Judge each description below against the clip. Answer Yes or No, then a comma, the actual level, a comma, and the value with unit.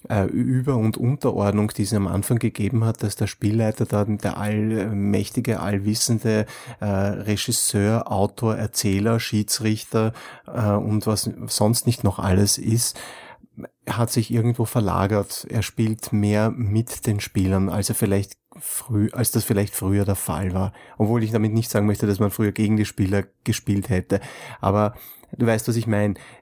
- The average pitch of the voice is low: Yes, low, 105 Hz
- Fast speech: No, average, 155 wpm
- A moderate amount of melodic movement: No, narrow, 2.2 semitones